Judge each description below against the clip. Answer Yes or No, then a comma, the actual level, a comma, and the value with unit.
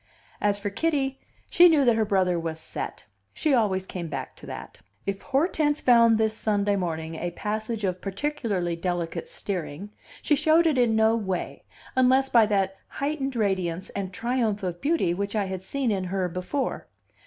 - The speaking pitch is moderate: No, high, 210 Hz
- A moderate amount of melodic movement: No, wide, 5.8 semitones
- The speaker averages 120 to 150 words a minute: No, average, 175 wpm